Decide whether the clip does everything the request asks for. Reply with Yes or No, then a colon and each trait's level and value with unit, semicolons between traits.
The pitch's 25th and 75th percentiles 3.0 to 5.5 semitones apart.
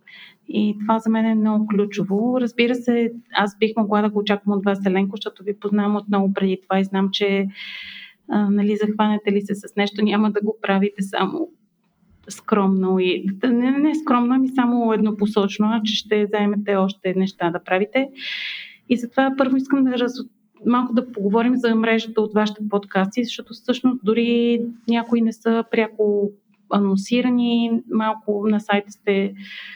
No: narrow, 2.6 semitones